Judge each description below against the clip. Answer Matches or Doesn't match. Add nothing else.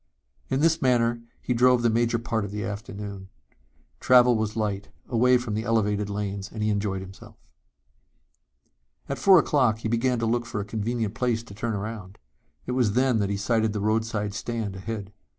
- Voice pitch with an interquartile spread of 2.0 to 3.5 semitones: Matches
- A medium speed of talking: Matches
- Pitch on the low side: Matches